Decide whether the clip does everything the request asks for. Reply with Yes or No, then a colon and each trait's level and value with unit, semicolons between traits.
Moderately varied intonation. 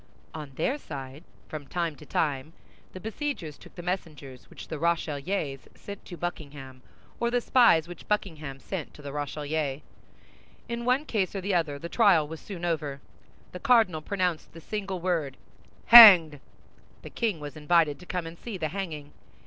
Yes: average, 4.7 semitones